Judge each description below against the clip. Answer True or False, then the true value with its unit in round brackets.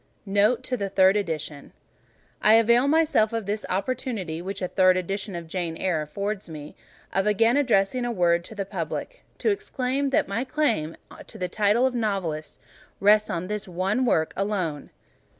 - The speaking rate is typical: True (170 wpm)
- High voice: True (200 Hz)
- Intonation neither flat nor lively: True (4.5 semitones)